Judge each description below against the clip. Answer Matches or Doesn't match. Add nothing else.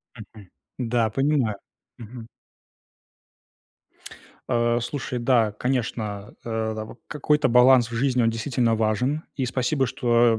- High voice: Doesn't match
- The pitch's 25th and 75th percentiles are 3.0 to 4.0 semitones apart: Doesn't match